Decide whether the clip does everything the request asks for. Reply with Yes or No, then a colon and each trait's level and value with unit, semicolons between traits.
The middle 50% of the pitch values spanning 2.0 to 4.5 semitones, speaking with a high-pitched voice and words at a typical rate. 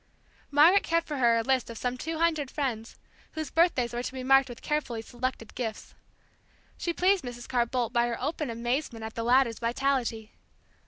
Yes: average, 3.8 semitones; very high, 255 Hz; average, 190 wpm